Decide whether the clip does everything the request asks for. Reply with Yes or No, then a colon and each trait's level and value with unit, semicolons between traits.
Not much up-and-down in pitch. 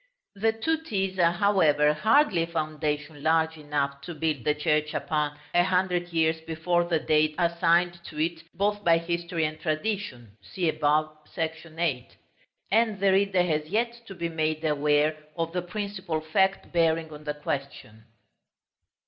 No: average, 3.0 semitones